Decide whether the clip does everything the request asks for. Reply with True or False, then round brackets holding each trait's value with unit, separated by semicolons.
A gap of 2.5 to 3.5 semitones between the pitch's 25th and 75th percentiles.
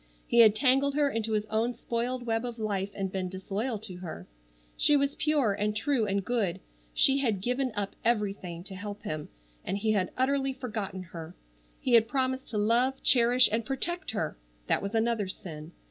False (4.4 semitones)